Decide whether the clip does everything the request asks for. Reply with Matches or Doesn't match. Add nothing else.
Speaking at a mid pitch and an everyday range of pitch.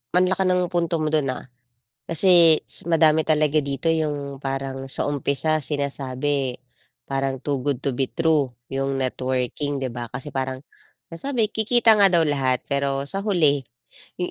Matches